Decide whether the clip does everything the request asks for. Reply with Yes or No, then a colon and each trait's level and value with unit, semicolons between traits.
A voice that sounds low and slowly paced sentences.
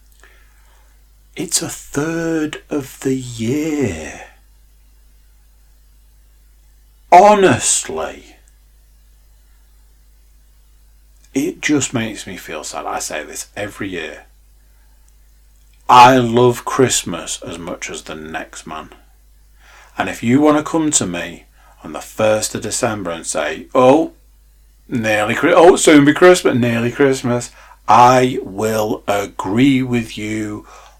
Yes: very low, 85 Hz; slow, 105 wpm